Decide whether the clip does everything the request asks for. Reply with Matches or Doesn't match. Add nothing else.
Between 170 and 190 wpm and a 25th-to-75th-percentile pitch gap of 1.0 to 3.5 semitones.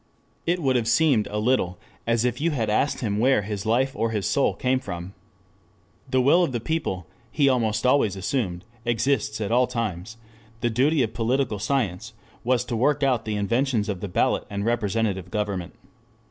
Doesn't match